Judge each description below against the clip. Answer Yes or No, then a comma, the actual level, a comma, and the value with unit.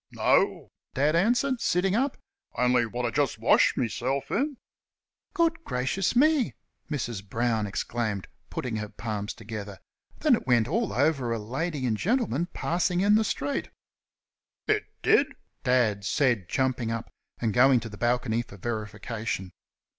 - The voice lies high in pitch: No, low, 125 Hz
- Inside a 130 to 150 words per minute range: Yes, average, 145 wpm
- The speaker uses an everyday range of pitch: No, wide, 7.6 semitones